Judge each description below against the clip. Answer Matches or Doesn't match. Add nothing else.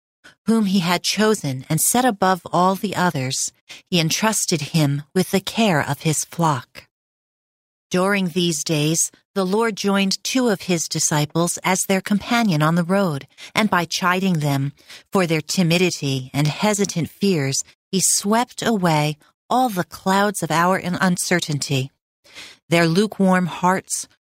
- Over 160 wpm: Doesn't match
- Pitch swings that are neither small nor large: Matches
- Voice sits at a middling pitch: Matches